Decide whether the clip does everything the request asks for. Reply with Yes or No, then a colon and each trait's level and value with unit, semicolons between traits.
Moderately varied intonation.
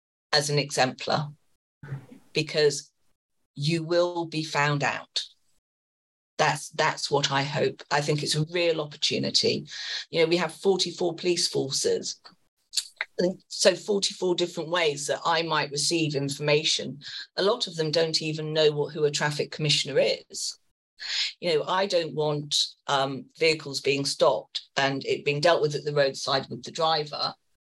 Yes: average, 3.0 semitones